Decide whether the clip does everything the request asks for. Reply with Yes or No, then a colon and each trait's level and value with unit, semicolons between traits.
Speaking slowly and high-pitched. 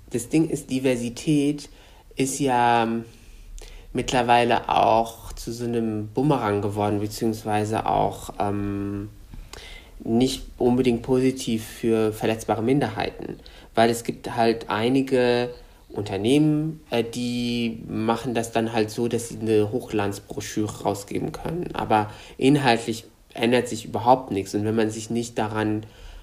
No: slow, 120 wpm; low, 115 Hz